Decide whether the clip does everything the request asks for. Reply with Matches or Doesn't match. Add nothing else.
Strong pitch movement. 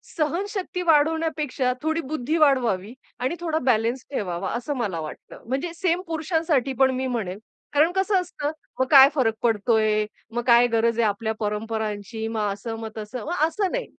Matches